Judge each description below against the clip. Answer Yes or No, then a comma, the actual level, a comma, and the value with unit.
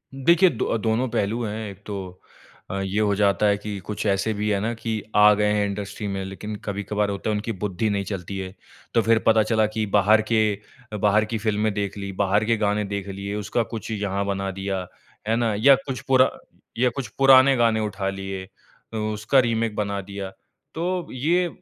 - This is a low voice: Yes, low, 105 Hz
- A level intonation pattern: Yes, narrow, 2.2 semitones